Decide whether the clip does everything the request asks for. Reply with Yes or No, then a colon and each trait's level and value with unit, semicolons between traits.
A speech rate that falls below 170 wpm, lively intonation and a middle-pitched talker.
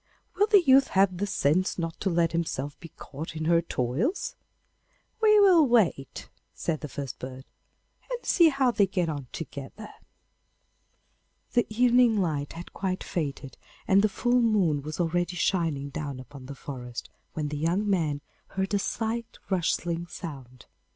Yes: average, 160 wpm; wide, 6.7 semitones; medium, 170 Hz